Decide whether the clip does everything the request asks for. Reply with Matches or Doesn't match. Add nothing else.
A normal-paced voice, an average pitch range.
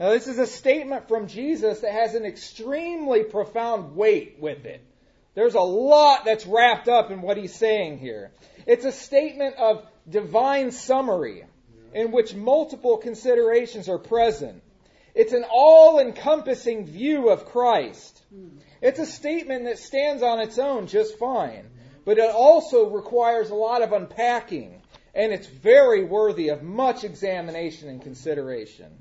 Matches